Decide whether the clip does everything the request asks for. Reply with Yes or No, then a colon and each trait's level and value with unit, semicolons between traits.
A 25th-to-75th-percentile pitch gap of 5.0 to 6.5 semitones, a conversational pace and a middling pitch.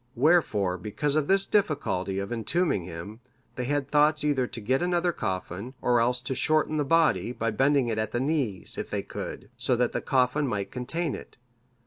No: wide, 5.5 semitones; average, 190 wpm; low, 125 Hz